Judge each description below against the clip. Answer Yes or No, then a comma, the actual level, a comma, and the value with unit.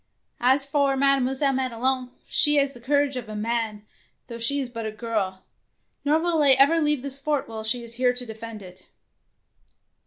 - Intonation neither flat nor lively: Yes, average, 3.5 semitones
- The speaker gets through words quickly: No, average, 185 wpm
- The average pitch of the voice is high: Yes, very high, 255 Hz